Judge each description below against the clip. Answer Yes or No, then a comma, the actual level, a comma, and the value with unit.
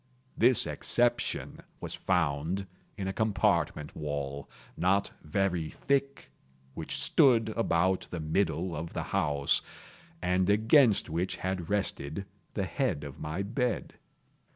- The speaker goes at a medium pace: No, slow, 120 wpm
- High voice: No, very low, 95 Hz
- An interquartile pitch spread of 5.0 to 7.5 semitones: Yes, wide, 5.4 semitones